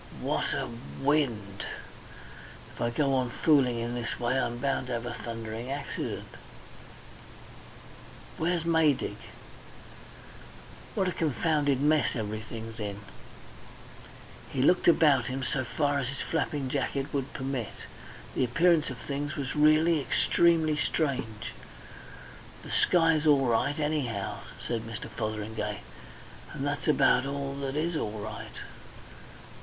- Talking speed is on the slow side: Yes, slow, 125 wpm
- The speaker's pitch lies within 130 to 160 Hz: Yes, low, 135 Hz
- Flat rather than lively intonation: No, average, 4.3 semitones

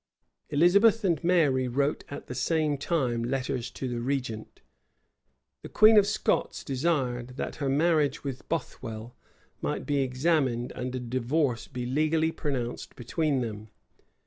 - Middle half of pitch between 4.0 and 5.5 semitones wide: Yes, average, 4.3 semitones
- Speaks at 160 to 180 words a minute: No, average, 140 wpm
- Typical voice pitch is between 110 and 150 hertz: Yes, low, 135 Hz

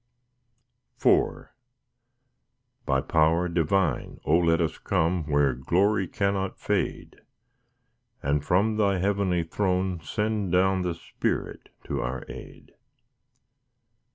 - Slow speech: Yes, slow, 100 wpm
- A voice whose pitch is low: Yes, very low, 90 Hz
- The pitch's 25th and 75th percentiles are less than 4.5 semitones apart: Yes, average, 3.3 semitones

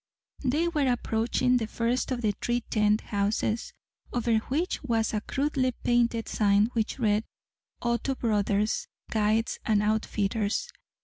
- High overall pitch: Yes, high, 225 Hz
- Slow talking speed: Yes, slow, 130 wpm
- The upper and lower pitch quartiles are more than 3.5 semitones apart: No, average, 2.7 semitones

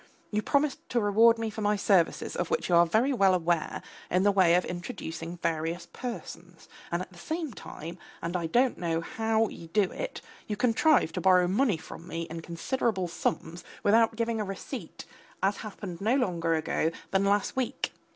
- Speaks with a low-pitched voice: No, high, 195 Hz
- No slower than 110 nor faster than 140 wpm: No, average, 190 wpm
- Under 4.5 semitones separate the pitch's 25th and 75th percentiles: No, average, 4.9 semitones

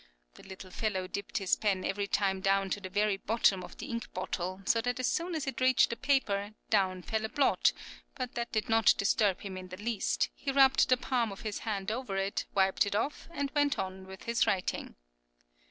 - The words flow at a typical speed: No, fast, 220 wpm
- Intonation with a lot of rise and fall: No, average, 3.9 semitones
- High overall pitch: Yes, high, 210 Hz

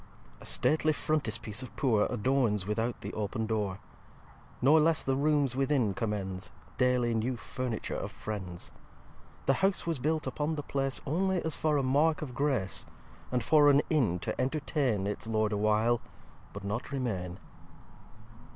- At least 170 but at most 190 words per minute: No, average, 160 wpm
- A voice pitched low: Yes, low, 125 Hz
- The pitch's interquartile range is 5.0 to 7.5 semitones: Yes, wide, 5.5 semitones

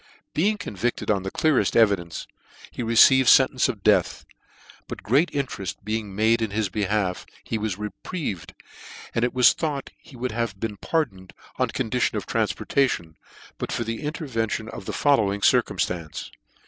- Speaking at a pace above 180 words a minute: No, average, 160 wpm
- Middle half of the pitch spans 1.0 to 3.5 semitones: No, average, 4.7 semitones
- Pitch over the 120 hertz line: No, low, 115 Hz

